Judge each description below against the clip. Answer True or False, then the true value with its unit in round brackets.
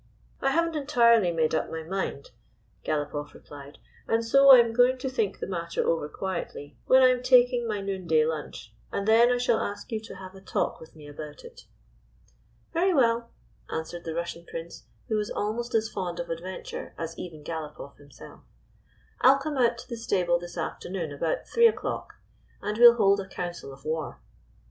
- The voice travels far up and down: True (6.6 semitones)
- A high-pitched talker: True (195 Hz)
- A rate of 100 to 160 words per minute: False (200 wpm)